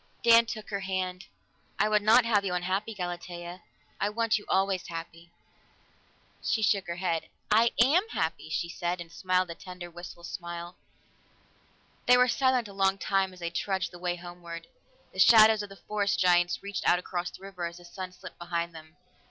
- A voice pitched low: No, medium, 185 Hz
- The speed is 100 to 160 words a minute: No, average, 185 wpm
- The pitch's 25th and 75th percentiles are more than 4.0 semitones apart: No, average, 3.0 semitones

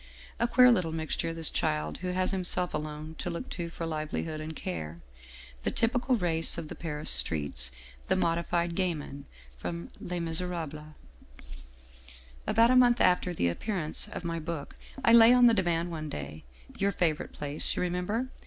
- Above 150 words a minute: Yes, average, 175 wpm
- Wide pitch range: No, average, 3.5 semitones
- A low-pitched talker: No, medium, 165 Hz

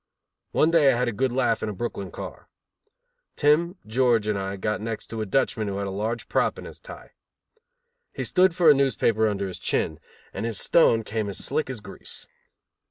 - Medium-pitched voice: No, low, 115 Hz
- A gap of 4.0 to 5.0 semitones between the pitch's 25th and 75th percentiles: Yes, average, 4.5 semitones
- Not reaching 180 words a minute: No, fast, 205 wpm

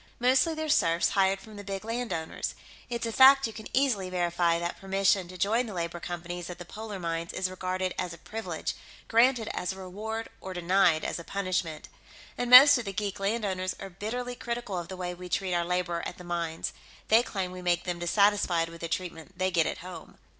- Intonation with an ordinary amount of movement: Yes, average, 3.9 semitones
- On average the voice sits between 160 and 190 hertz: Yes, medium, 185 Hz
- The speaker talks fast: Yes, fast, 210 wpm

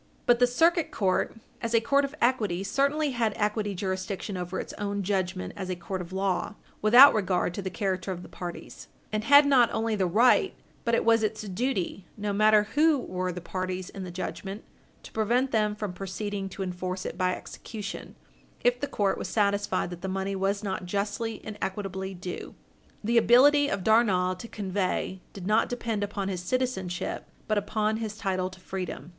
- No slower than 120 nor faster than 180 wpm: No, average, 190 wpm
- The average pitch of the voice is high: Yes, high, 205 Hz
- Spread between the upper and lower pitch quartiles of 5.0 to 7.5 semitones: No, average, 3.3 semitones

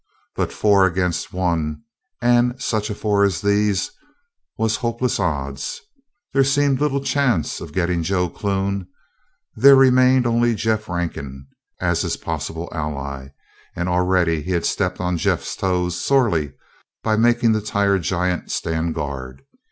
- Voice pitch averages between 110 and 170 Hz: No, very low, 95 Hz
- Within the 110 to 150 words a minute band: Yes, average, 140 wpm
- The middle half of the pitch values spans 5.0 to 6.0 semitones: Yes, wide, 5.4 semitones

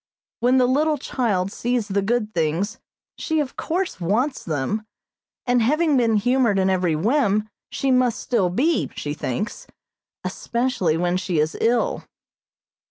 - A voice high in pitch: Yes, high, 225 Hz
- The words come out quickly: No, average, 145 wpm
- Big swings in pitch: Yes, wide, 5.7 semitones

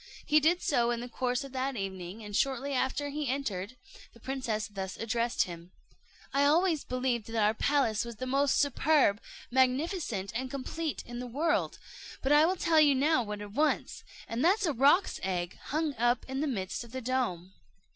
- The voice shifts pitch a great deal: No, average, 4.5 semitones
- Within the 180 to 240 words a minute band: Yes, average, 195 wpm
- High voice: Yes, very high, 255 Hz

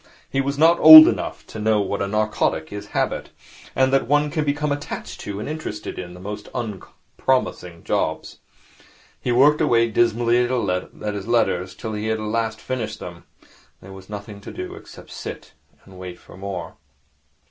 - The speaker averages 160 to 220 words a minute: Yes, average, 170 wpm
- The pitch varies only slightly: No, average, 4.7 semitones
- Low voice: Yes, low, 110 Hz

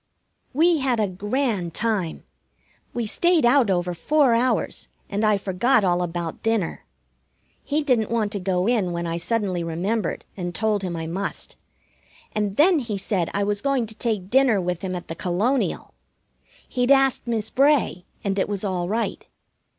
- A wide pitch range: No, average, 5.0 semitones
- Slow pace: No, average, 170 wpm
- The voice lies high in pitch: Yes, high, 205 Hz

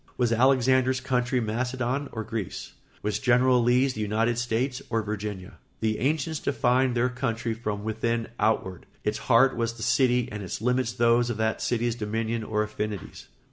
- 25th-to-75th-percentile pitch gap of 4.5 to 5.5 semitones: No, narrow, 2.4 semitones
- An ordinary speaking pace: Yes, average, 165 wpm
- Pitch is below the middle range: Yes, low, 115 Hz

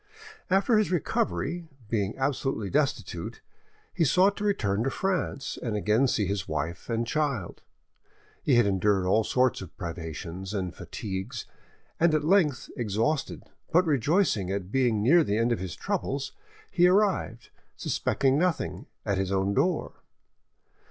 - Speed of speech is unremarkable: Yes, average, 145 wpm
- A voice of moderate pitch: No, low, 120 Hz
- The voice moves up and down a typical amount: No, wide, 8.0 semitones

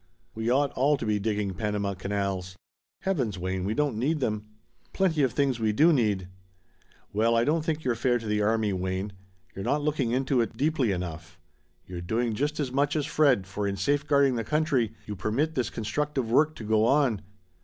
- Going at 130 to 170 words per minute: No, average, 195 wpm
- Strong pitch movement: Yes, wide, 5.7 semitones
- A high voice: No, low, 115 Hz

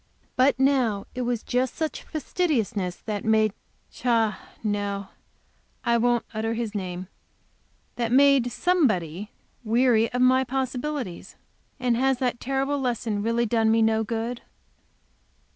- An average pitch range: Yes, average, 3.0 semitones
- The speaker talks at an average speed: No, slow, 125 wpm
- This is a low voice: No, high, 235 Hz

